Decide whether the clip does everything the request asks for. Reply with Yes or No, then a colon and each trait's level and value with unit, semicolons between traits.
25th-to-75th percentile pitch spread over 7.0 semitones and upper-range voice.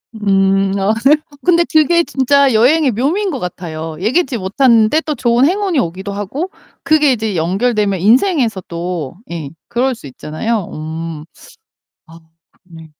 Yes: wide, 7.8 semitones; high, 220 Hz